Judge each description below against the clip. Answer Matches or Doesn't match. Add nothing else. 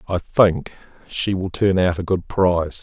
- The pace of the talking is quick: Doesn't match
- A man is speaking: Matches